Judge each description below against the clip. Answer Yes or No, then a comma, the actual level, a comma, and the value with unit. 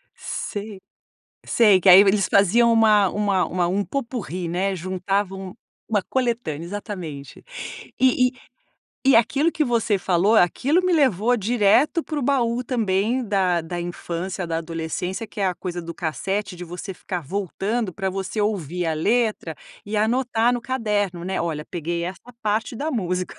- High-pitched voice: Yes, high, 200 Hz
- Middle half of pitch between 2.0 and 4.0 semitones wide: No, average, 4.5 semitones